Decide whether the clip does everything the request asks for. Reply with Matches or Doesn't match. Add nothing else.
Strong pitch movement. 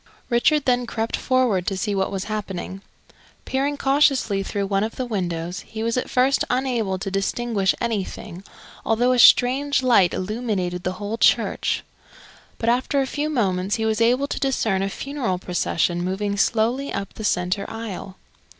Doesn't match